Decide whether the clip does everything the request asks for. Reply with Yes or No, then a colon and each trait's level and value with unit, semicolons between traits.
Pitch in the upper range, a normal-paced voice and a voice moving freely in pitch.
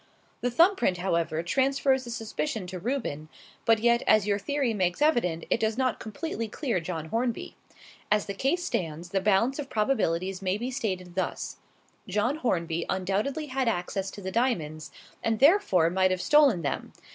Yes: high, 210 Hz; average, 170 wpm; wide, 6.1 semitones